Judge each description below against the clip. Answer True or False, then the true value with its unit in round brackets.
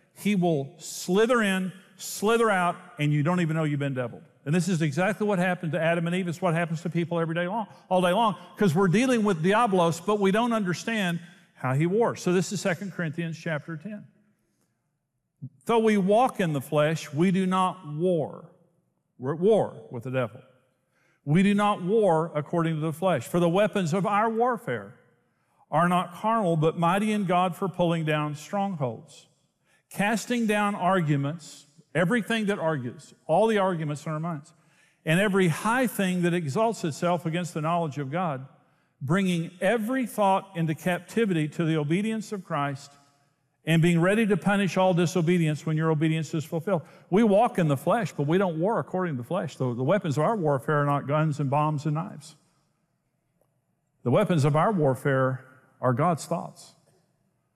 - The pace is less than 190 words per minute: True (180 wpm)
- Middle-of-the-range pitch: True (175 Hz)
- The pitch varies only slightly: False (3.9 semitones)